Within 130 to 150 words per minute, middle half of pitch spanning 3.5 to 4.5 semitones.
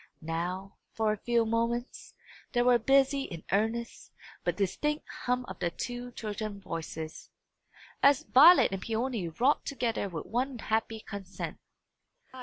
Yes: average, 140 wpm; average, 4.2 semitones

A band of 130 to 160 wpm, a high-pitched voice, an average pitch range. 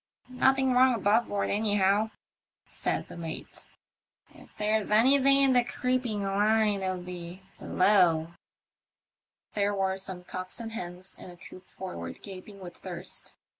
Yes: average, 140 wpm; high, 200 Hz; average, 3.3 semitones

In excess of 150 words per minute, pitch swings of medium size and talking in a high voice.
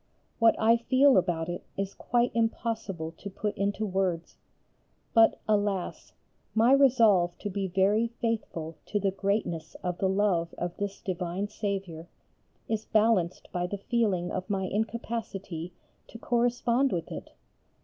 No: average, 140 wpm; average, 3.9 semitones; high, 200 Hz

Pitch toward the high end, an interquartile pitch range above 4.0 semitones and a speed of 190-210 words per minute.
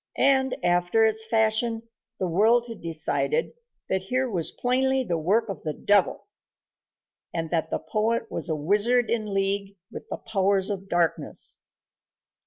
No: high, 205 Hz; average, 4.7 semitones; average, 150 wpm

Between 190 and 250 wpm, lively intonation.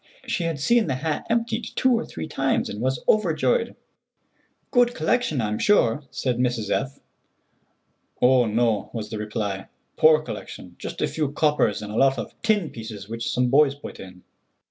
No: average, 170 wpm; wide, 6.8 semitones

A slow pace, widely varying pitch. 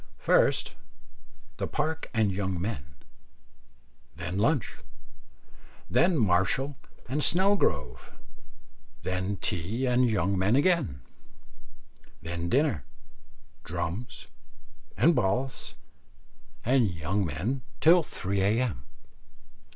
Yes: slow, 90 wpm; wide, 7.2 semitones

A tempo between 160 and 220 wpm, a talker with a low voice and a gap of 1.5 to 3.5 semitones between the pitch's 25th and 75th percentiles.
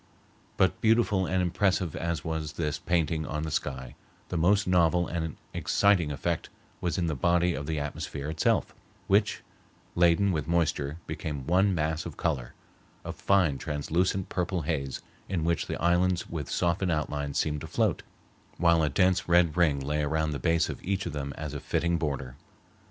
Yes: average, 170 wpm; very low, 85 Hz; average, 3.0 semitones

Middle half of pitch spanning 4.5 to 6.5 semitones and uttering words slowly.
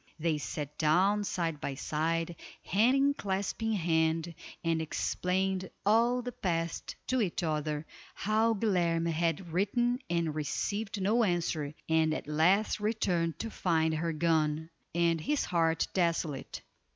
No: average, 4.1 semitones; slow, 130 wpm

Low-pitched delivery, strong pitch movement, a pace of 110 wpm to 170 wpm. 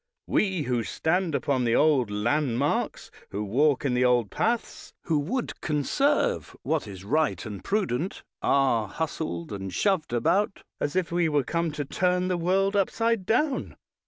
No: medium, 155 Hz; wide, 7.1 semitones; average, 160 wpm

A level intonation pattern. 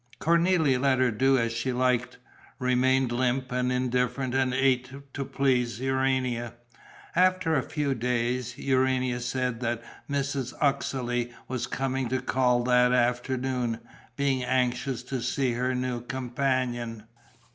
Yes: narrow, 1.4 semitones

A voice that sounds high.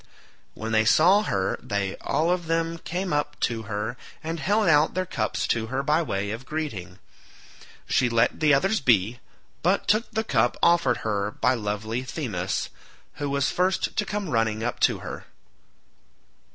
No: low, 135 Hz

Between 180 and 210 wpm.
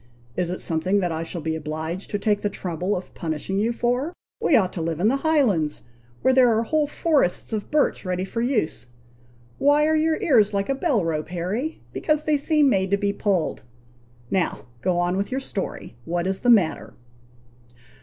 Yes: average, 195 wpm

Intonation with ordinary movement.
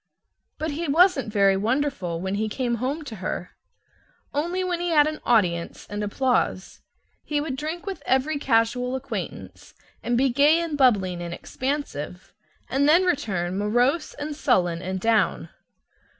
No: wide, 6.7 semitones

